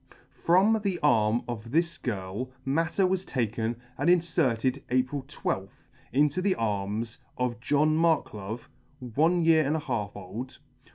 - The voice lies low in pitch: Yes, low, 130 Hz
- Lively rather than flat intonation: Yes, wide, 6.4 semitones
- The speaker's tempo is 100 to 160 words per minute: Yes, slow, 135 wpm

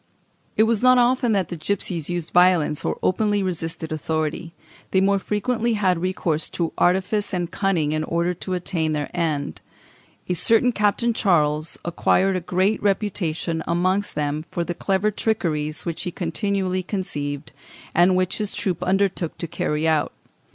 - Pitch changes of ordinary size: Yes, average, 3.6 semitones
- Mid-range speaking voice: Yes, medium, 180 Hz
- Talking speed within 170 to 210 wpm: No, average, 160 wpm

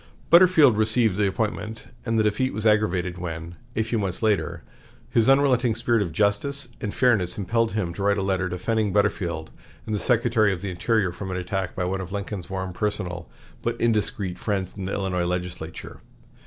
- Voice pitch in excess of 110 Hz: No, low, 100 Hz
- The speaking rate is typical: Yes, average, 185 wpm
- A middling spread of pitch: Yes, average, 3.4 semitones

